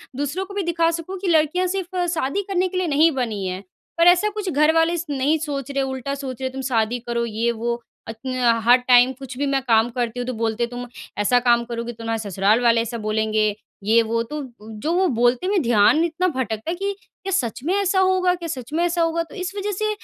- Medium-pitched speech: No, very high, 270 Hz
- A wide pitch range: Yes, wide, 6.5 semitones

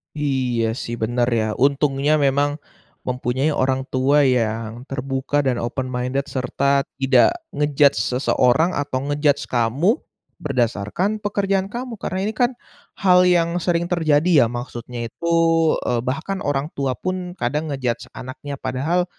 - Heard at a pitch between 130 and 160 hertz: Yes, medium, 140 Hz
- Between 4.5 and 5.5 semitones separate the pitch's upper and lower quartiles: Yes, average, 4.8 semitones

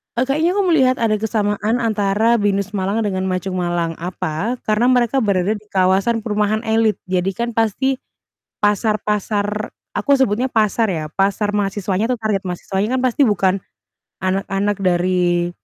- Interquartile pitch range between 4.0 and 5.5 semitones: No, average, 3.1 semitones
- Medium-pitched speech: No, high, 205 Hz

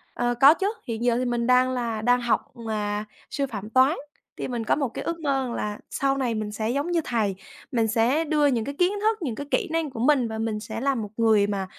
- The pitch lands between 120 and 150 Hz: No, high, 240 Hz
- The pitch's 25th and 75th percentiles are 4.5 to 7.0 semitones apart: No, average, 4.0 semitones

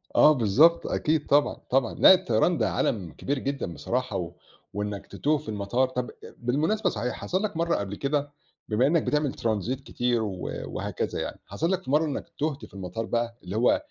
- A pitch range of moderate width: No, wide, 5.7 semitones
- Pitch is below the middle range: Yes, low, 130 Hz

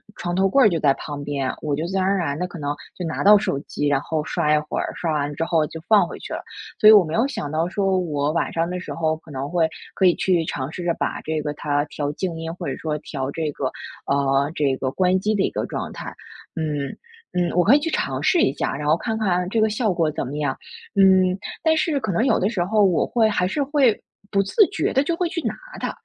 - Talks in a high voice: No, medium, 175 Hz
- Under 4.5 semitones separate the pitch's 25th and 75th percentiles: No, average, 5.0 semitones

